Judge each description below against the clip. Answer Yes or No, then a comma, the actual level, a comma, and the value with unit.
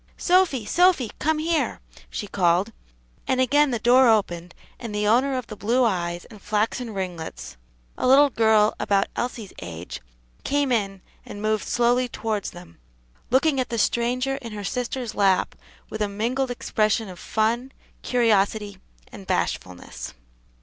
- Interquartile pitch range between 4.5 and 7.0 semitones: No, average, 3.9 semitones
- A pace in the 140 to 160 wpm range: Yes, average, 150 wpm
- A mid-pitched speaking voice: No, high, 225 Hz